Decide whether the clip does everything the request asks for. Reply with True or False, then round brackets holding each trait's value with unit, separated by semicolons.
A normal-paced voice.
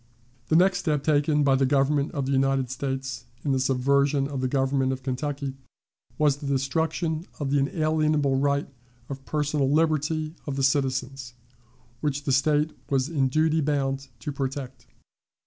True (160 wpm)